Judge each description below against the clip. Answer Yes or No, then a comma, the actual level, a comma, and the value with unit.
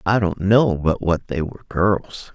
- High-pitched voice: No, very low, 95 Hz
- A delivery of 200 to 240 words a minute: Yes, fast, 205 wpm